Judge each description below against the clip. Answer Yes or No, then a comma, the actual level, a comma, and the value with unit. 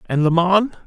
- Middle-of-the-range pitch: Yes, medium, 180 Hz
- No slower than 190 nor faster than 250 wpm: Yes, fast, 210 wpm